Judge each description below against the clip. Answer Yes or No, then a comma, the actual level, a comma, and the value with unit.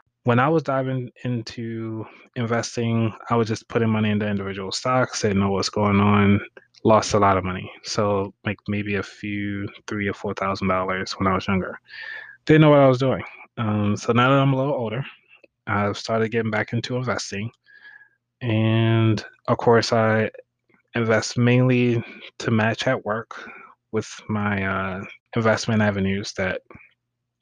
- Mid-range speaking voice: No, low, 110 Hz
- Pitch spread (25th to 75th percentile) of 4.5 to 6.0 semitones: No, average, 2.9 semitones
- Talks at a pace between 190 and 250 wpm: No, average, 160 wpm